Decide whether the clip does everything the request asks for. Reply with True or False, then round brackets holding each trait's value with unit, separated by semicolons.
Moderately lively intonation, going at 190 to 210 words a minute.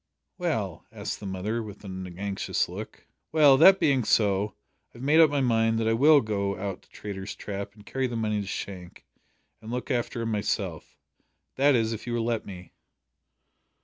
True (3.7 semitones; 195 wpm)